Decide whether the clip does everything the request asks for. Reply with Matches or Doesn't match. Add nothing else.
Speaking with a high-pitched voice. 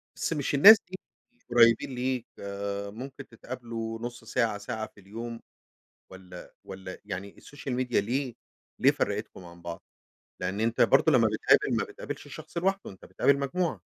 Doesn't match